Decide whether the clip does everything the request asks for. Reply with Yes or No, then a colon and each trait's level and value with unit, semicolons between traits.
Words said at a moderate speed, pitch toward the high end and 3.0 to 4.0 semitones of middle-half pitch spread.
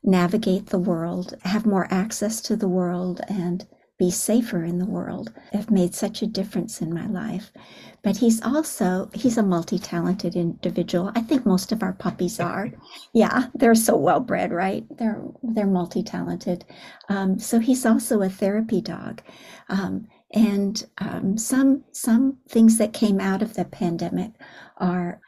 Yes: average, 155 wpm; high, 200 Hz; average, 3.6 semitones